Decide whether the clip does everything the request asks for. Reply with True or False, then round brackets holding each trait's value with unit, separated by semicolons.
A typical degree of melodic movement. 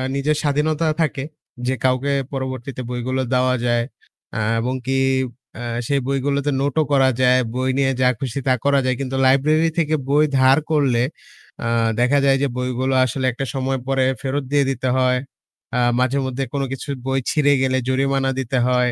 False (1.5 semitones)